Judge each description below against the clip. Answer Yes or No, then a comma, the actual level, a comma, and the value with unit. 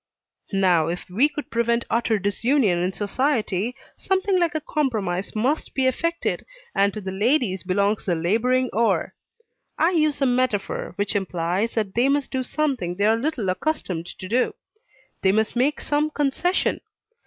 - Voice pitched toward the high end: Yes, high, 230 Hz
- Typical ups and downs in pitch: No, wide, 6.4 semitones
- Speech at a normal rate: Yes, average, 160 wpm